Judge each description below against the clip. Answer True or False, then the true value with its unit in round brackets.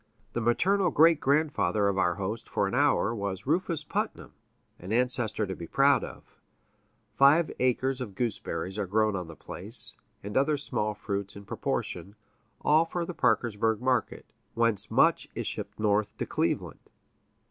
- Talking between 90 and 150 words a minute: False (160 wpm)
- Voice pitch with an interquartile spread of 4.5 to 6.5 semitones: True (5.5 semitones)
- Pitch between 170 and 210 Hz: False (115 Hz)